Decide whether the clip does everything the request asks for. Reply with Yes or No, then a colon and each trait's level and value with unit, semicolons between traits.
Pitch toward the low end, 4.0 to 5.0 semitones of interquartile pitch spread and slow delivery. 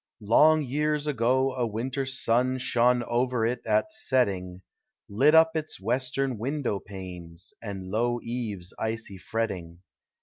Yes: low, 120 Hz; average, 4.5 semitones; slow, 130 wpm